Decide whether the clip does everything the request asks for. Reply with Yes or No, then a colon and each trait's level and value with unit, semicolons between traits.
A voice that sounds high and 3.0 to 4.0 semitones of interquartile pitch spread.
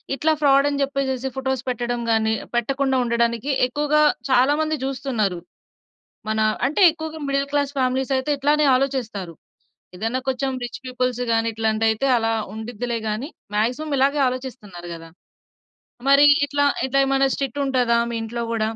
Yes: very high, 255 Hz; average, 3.3 semitones